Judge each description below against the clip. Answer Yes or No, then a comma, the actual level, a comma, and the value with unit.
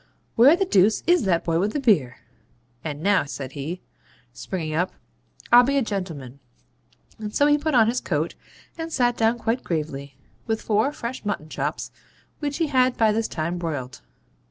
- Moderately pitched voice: No, high, 210 Hz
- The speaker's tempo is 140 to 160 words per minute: No, average, 180 wpm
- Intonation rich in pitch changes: Yes, wide, 7.8 semitones